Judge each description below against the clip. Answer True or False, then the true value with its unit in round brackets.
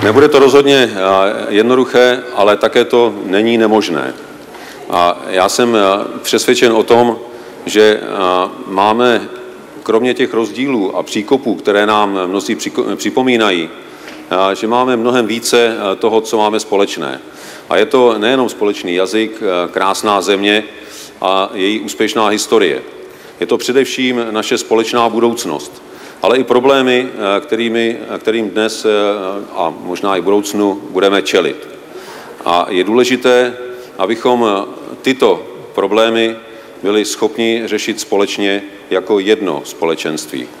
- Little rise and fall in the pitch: False (3.3 semitones)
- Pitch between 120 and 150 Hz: False (110 Hz)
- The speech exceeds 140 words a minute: False (115 wpm)